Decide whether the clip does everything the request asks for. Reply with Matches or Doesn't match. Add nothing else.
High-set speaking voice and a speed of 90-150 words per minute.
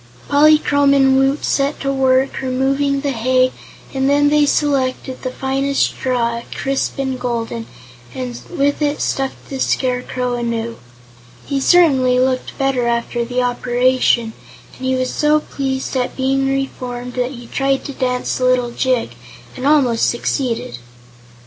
Matches